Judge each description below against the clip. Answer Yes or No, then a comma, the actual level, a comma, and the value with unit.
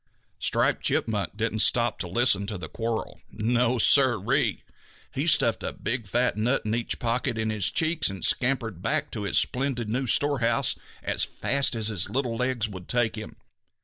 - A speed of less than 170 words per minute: No, average, 180 wpm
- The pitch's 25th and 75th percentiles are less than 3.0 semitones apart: Yes, narrow, 2.6 semitones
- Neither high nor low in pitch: No, low, 115 Hz